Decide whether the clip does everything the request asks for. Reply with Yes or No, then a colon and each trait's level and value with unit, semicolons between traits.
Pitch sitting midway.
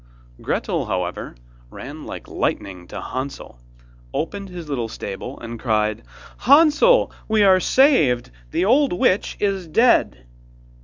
Yes: medium, 160 Hz